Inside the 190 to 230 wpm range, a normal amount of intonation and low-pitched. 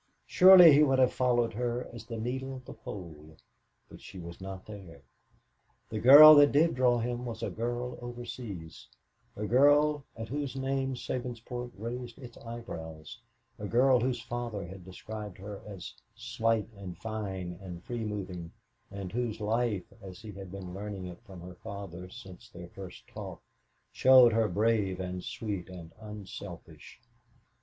No: average, 155 wpm; average, 4.6 semitones; low, 110 Hz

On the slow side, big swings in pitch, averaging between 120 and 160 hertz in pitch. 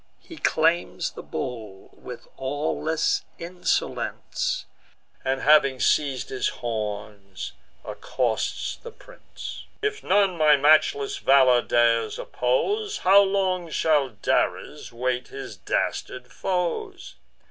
Yes: slow, 105 wpm; wide, 6.7 semitones; medium, 140 Hz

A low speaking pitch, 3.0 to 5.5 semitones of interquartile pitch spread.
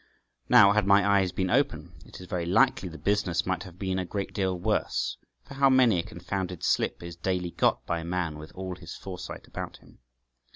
No: very low, 95 Hz; narrow, 2.4 semitones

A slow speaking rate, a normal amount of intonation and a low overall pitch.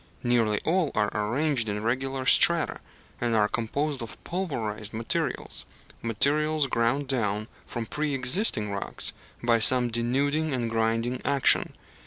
Yes: slow, 130 wpm; average, 4.0 semitones; low, 120 Hz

